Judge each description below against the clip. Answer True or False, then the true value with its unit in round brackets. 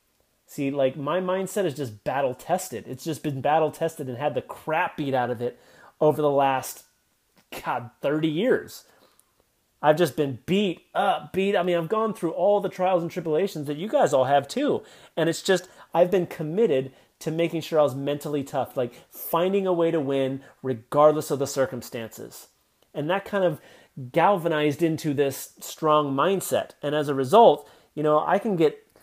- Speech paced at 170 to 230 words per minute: True (185 wpm)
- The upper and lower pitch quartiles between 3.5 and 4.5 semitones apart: True (3.8 semitones)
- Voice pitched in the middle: True (155 Hz)